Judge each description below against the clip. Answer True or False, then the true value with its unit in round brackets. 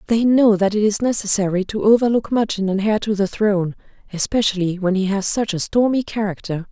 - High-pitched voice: True (205 Hz)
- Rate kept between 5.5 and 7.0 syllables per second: True (5.7 syllables/s)